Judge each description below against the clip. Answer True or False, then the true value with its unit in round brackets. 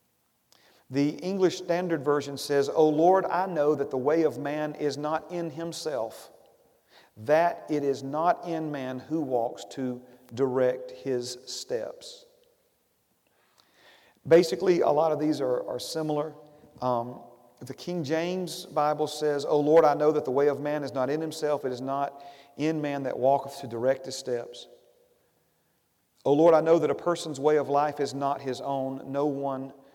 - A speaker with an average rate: True (170 wpm)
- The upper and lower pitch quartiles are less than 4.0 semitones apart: True (3.2 semitones)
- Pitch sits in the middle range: True (145 Hz)